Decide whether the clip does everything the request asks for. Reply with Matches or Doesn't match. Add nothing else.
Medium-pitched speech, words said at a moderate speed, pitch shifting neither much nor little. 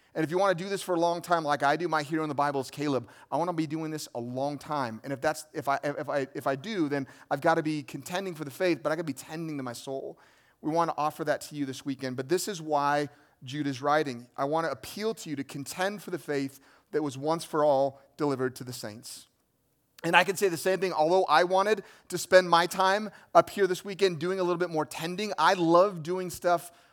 Doesn't match